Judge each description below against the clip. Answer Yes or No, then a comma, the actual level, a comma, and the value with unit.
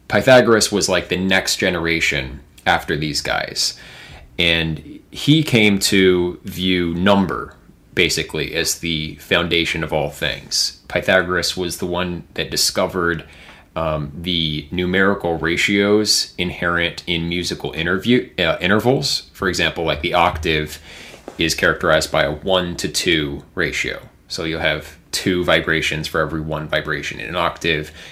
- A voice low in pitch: Yes, very low, 85 Hz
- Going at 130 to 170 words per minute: Yes, slow, 135 wpm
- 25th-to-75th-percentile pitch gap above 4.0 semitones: No, average, 3.2 semitones